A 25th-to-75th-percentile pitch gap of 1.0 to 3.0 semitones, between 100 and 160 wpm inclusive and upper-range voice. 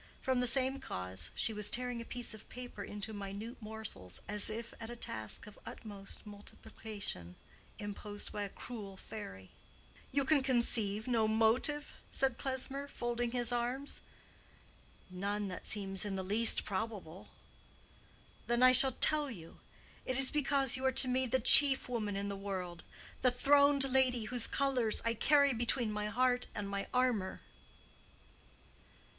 No: average, 3.9 semitones; average, 150 wpm; high, 230 Hz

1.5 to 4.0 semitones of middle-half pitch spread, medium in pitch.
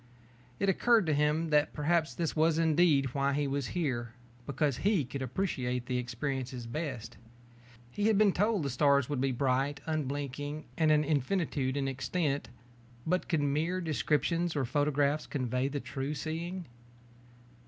Yes: average, 3.3 semitones; medium, 145 Hz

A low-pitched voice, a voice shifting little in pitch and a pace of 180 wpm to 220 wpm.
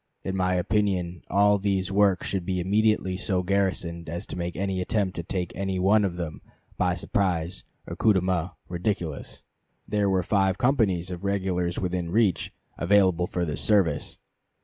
No: very low, 95 Hz; narrow, 2.2 semitones; average, 170 wpm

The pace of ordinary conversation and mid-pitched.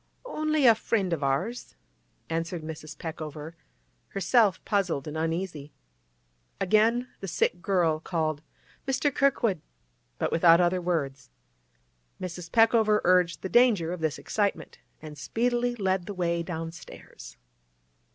No: slow, 120 wpm; medium, 175 Hz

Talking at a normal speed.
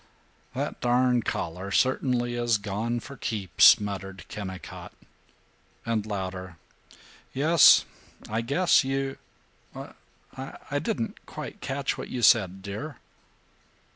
No: slow, 105 wpm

